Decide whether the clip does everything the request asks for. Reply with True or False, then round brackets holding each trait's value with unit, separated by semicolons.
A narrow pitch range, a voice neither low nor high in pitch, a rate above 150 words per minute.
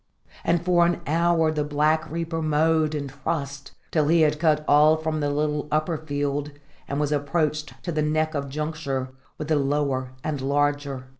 True (1.7 semitones; 150 Hz; 175 wpm)